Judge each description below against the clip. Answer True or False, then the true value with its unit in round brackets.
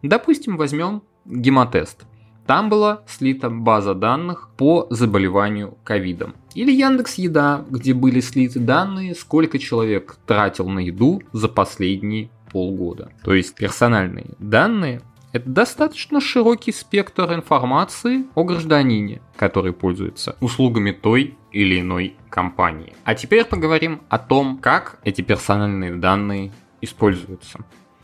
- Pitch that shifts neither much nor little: False (8.2 semitones)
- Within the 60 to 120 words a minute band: True (115 wpm)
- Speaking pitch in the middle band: False (125 Hz)